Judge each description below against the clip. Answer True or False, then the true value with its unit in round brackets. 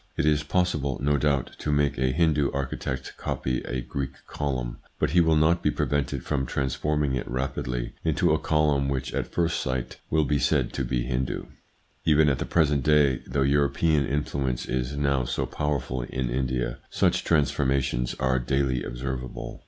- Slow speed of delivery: False (170 wpm)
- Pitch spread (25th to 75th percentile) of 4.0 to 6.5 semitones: False (2.4 semitones)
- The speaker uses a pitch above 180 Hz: False (70 Hz)